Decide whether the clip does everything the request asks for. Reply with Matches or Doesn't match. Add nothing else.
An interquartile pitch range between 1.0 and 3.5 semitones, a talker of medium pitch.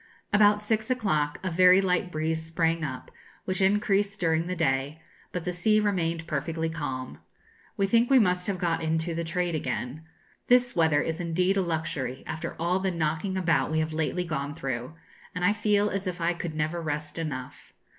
Matches